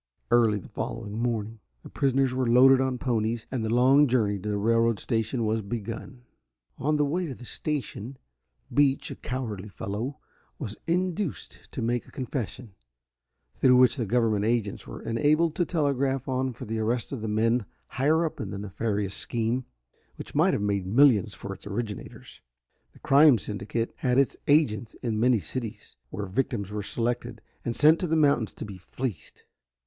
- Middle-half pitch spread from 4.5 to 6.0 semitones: No, average, 3.8 semitones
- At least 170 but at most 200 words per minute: Yes, average, 175 wpm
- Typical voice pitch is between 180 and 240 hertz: No, low, 120 Hz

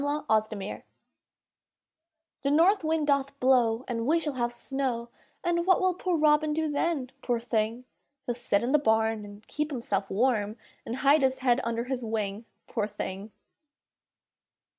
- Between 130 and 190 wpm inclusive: Yes, average, 160 wpm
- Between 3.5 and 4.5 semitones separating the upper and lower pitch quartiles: No, average, 4.9 semitones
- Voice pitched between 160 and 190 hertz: No, very high, 250 Hz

